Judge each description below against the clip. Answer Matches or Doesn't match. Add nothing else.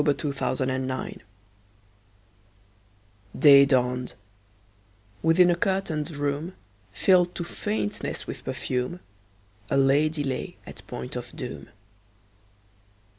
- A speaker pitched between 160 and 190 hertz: Doesn't match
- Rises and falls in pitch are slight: Doesn't match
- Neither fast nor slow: Doesn't match